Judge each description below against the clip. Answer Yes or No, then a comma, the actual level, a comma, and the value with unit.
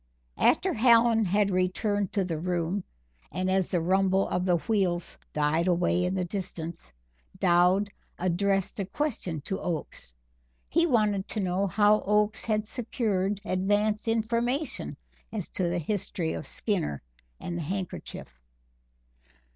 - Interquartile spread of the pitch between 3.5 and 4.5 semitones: No, average, 3.1 semitones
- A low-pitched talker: No, high, 190 Hz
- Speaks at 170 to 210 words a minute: No, slow, 135 wpm